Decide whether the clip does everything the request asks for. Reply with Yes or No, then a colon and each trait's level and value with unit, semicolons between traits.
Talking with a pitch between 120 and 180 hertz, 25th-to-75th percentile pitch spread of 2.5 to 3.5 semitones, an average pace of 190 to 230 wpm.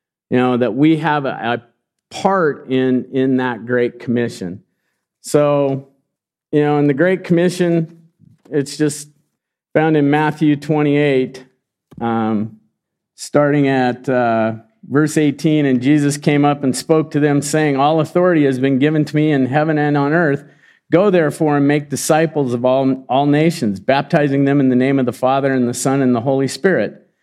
No: medium, 140 Hz; average, 2.9 semitones; average, 170 wpm